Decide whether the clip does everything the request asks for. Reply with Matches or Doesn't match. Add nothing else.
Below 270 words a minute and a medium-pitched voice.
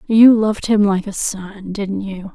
Doesn't match